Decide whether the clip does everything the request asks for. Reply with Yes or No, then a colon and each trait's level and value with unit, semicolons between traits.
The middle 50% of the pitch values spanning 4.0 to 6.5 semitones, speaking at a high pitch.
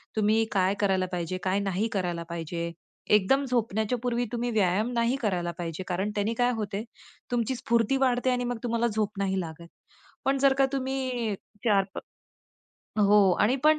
Yes: average, 4.3 semitones; high, 215 Hz